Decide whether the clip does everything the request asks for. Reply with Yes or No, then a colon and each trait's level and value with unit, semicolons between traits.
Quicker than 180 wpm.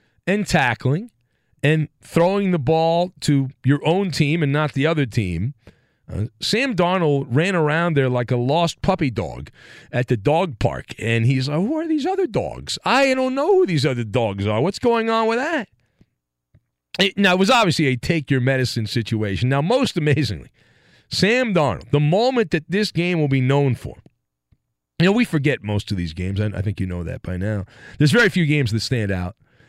Yes: average, 200 wpm